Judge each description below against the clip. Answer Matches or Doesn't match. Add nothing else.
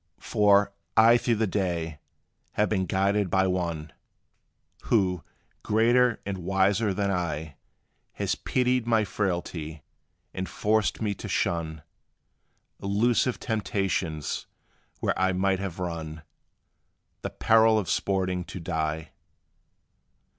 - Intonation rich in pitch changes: Doesn't match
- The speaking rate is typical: Doesn't match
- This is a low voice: Matches